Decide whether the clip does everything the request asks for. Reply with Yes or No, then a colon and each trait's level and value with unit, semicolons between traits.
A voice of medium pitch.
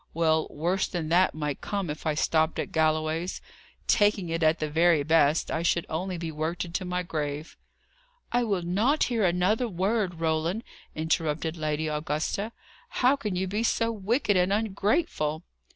Yes: medium, 170 Hz